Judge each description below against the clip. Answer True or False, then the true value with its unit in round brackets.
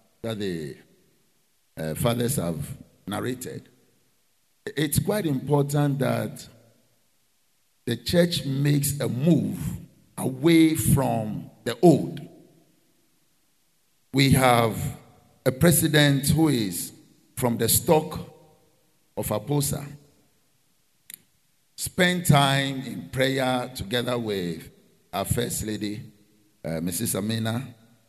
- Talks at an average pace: False (90 wpm)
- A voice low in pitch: True (130 Hz)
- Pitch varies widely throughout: False (4.5 semitones)